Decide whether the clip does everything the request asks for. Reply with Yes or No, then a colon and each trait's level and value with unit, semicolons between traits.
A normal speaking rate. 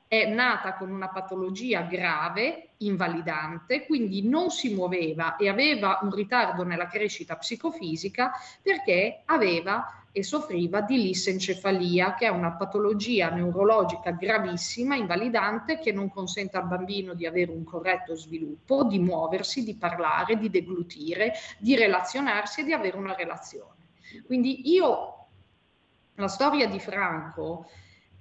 Yes: average, 130 wpm